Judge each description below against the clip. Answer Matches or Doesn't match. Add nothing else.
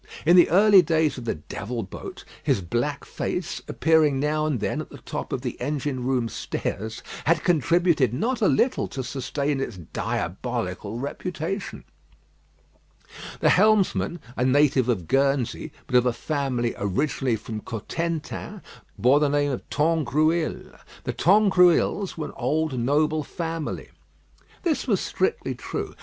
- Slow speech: Doesn't match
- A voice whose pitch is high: Doesn't match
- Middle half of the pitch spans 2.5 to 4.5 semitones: Doesn't match